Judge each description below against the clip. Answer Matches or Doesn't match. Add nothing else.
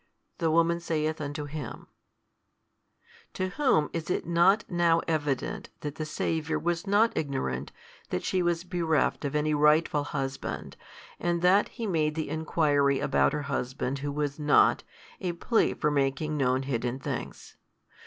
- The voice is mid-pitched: Matches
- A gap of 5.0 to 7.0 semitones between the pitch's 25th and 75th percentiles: Doesn't match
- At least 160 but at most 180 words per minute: Doesn't match